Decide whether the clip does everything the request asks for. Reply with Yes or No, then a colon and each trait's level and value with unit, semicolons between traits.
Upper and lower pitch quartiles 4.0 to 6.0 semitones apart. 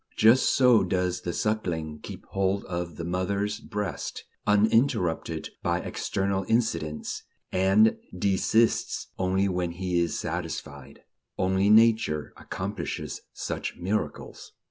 No: average, 3.5 semitones